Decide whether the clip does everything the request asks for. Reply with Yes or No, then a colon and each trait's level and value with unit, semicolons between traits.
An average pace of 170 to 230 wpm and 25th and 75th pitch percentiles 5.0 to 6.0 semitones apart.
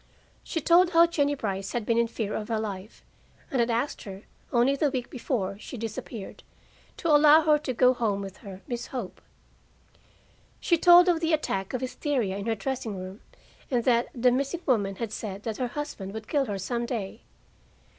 Yes: average, 195 wpm; wide, 5.4 semitones